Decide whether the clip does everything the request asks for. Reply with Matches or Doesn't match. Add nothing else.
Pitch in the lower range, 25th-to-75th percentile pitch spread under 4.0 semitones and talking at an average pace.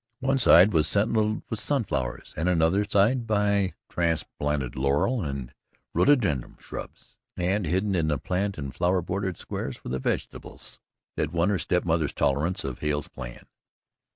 Doesn't match